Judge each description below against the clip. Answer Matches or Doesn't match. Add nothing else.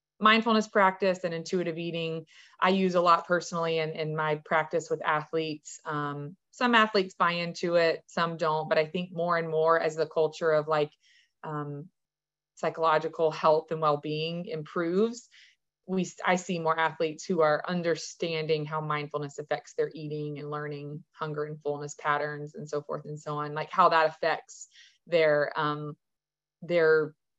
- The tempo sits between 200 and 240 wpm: Doesn't match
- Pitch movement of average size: Doesn't match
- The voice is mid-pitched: Matches